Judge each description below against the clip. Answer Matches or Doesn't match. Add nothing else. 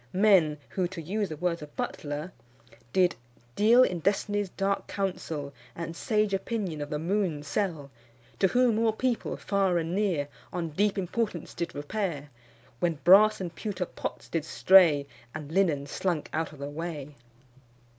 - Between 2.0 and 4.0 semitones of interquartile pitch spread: Doesn't match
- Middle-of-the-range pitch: Matches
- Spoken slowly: Doesn't match